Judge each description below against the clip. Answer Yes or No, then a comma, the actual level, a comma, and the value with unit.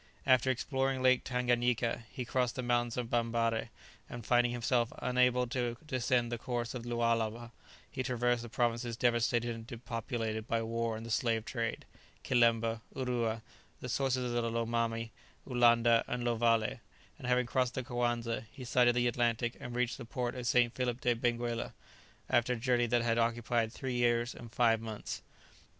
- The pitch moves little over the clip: Yes, narrow, 1.1 semitones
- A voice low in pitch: Yes, low, 120 Hz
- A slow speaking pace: No, average, 170 wpm